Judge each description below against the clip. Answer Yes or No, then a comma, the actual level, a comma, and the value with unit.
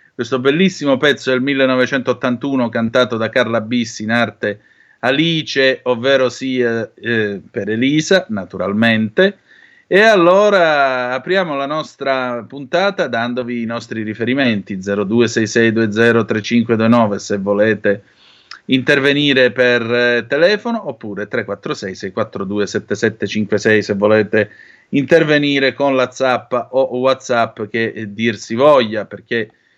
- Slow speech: Yes, slow, 105 wpm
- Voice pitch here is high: No, low, 120 Hz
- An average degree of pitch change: Yes, average, 3.6 semitones